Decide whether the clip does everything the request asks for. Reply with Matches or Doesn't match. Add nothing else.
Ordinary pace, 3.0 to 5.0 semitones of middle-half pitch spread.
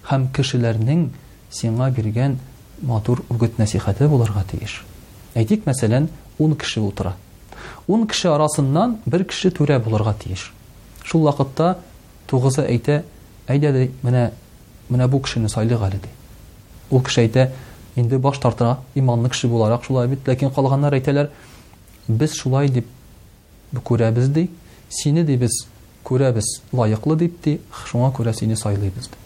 Matches